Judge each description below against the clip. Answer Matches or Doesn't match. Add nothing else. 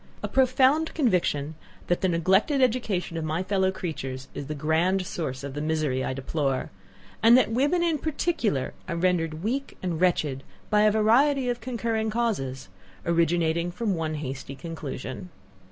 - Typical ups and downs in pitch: Doesn't match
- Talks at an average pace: Matches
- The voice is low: Doesn't match